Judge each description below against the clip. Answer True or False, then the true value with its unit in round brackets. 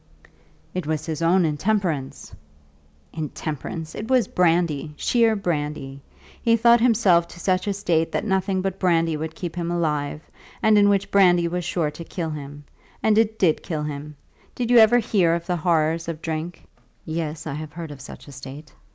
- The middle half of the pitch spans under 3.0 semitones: False (3.9 semitones)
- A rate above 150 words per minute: True (180 wpm)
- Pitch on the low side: False (170 Hz)